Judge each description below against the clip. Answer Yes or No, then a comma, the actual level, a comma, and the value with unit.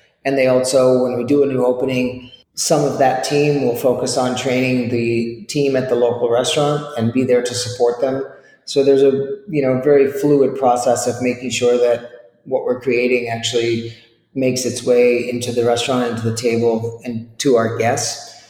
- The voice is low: Yes, low, 125 Hz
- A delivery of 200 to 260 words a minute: No, average, 190 wpm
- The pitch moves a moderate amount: No, narrow, 2.0 semitones